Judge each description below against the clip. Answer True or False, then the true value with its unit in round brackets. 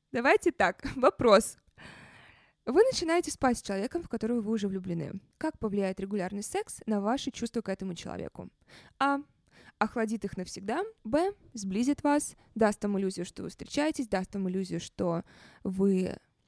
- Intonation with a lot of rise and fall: True (6.5 semitones)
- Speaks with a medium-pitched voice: False (215 Hz)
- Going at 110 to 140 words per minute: False (150 wpm)